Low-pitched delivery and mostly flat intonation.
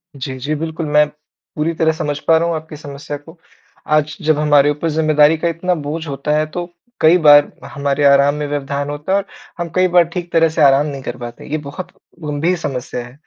No: medium, 150 Hz; narrow, 2.2 semitones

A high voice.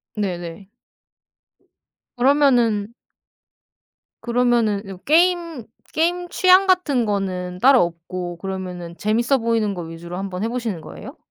Yes: high, 215 Hz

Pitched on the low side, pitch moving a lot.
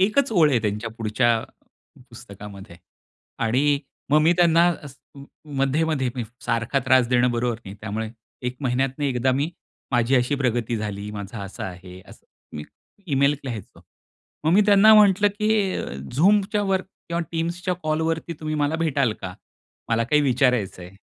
Yes: low, 130 Hz; wide, 6.1 semitones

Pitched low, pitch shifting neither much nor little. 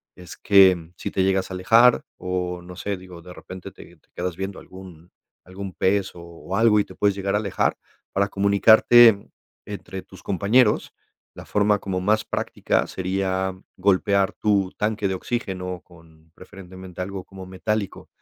No: very low, 95 Hz; narrow, 1.7 semitones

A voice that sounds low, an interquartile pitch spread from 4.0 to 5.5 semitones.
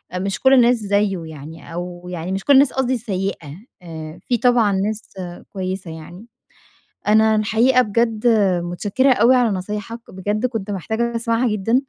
No: high, 210 Hz; average, 4.3 semitones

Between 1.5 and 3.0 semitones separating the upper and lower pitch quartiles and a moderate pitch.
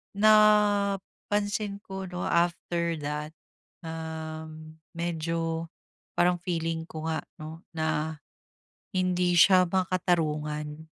Yes: average, 2.7 semitones; medium, 170 Hz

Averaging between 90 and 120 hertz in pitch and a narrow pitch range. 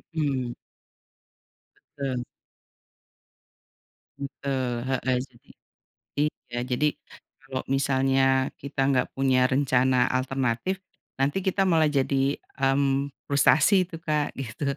No: low, 135 Hz; narrow, 1.6 semitones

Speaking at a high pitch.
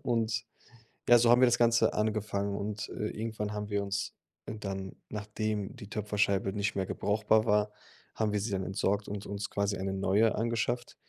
No: low, 105 Hz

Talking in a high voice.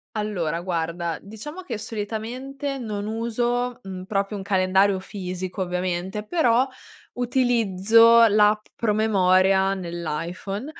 Yes: high, 205 Hz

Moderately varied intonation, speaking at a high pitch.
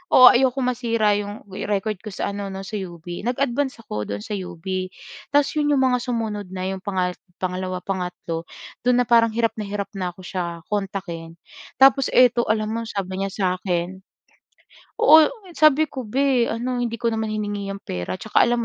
Yes: average, 4.5 semitones; high, 210 Hz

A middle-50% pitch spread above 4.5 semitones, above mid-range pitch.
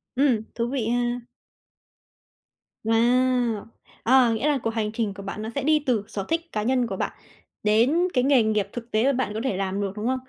No: average, 3.2 semitones; high, 235 Hz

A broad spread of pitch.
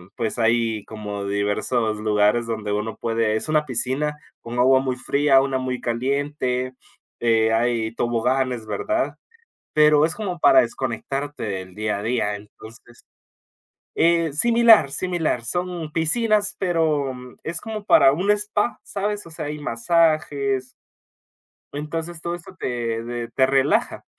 Yes: wide, 6.0 semitones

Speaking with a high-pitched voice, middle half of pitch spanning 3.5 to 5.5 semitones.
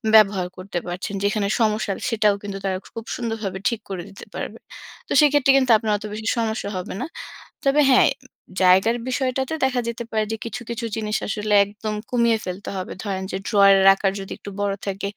No: high, 215 Hz; average, 3.1 semitones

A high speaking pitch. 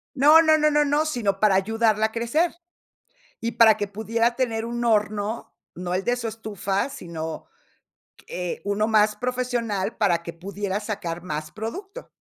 Yes: high, 220 Hz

